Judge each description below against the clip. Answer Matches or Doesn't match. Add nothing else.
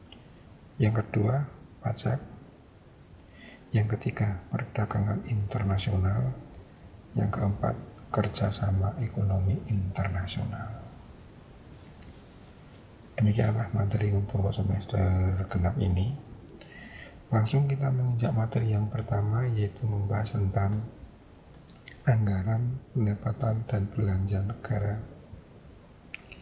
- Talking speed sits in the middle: Doesn't match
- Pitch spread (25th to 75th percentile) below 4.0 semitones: Matches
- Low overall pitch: Matches